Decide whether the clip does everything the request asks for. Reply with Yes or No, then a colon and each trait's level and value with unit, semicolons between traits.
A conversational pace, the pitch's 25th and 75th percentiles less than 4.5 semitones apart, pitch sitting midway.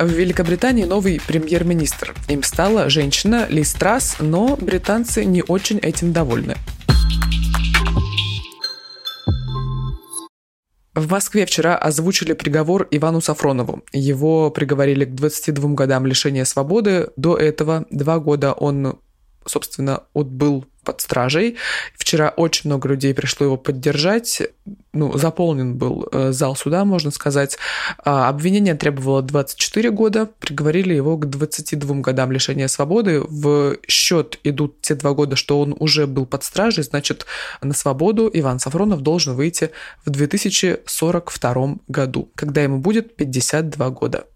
Yes: average, 120 wpm; average, 4.0 semitones; medium, 150 Hz